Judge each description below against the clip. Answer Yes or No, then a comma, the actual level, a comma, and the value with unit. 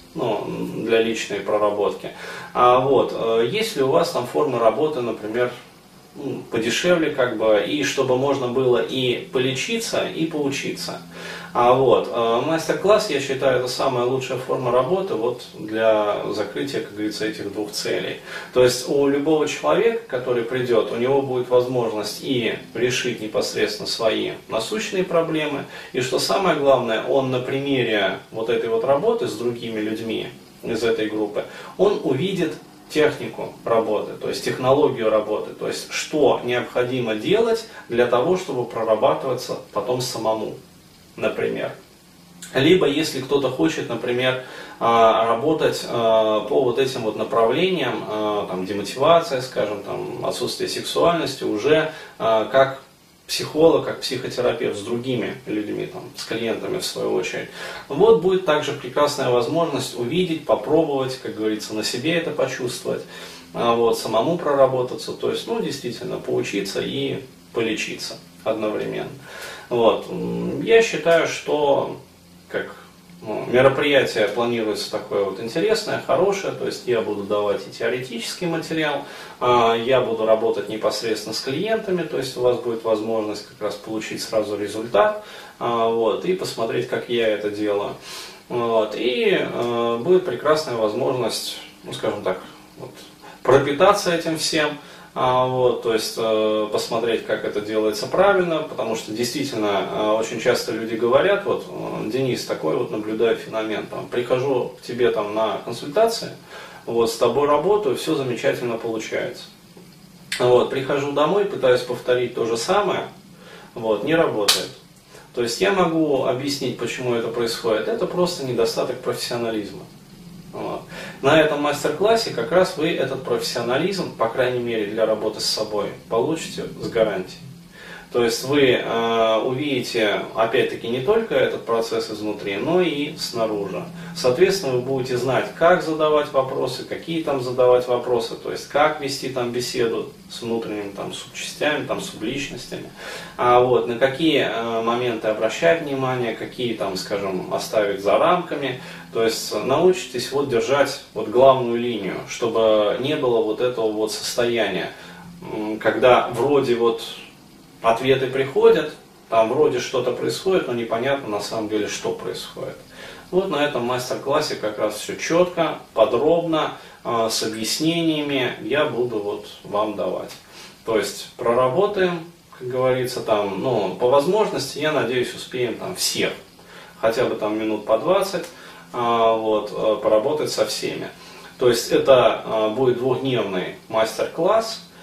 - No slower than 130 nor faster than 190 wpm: Yes, average, 135 wpm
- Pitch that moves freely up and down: Yes, wide, 6.3 semitones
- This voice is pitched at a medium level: No, low, 130 Hz